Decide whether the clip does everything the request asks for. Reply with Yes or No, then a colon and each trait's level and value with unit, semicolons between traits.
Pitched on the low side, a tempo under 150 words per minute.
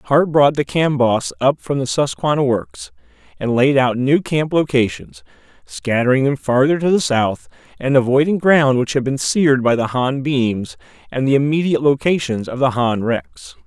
No: low, 130 Hz; average, 175 wpm